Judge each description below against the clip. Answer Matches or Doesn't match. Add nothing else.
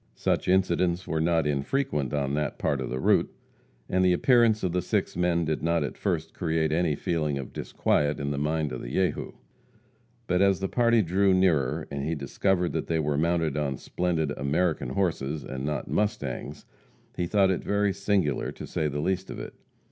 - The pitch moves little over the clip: Doesn't match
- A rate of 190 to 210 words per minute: Matches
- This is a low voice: Matches